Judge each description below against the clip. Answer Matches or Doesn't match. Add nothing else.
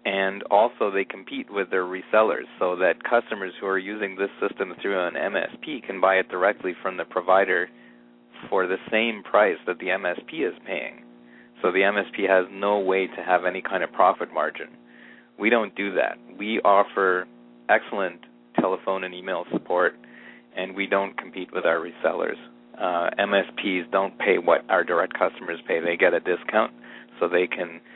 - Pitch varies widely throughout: Matches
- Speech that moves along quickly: Doesn't match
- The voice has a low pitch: Matches